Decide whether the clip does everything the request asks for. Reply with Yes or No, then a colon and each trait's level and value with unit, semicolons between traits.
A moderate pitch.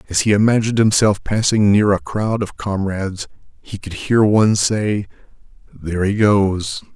No: low, 100 Hz